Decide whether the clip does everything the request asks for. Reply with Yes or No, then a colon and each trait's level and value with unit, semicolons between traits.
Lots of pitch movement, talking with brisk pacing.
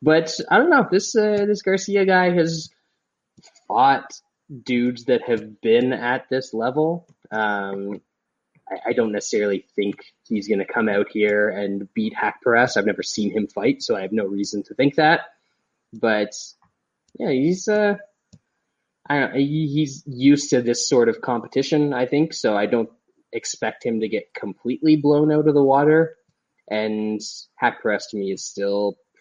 No: wide, 6.7 semitones; average, 170 wpm